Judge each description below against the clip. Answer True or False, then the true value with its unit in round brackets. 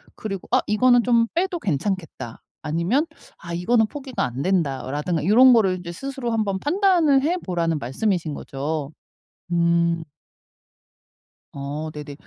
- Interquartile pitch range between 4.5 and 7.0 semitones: False (7.5 semitones)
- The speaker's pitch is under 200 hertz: True (185 Hz)